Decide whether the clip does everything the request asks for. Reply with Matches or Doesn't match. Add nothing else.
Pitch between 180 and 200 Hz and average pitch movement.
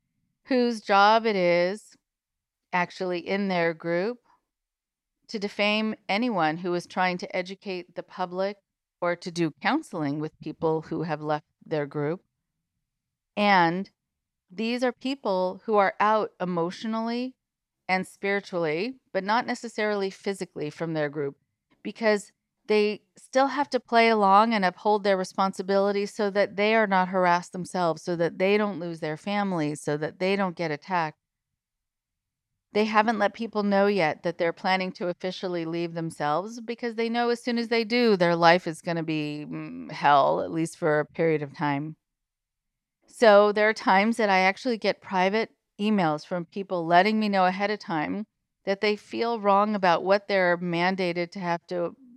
Matches